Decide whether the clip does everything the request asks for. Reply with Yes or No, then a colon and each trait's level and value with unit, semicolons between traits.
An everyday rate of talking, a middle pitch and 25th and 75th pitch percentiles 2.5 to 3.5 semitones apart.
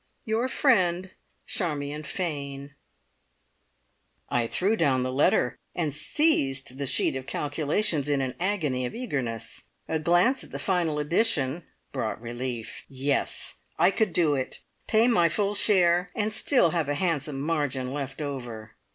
No: average, 145 wpm; medium, 150 Hz; average, 5.2 semitones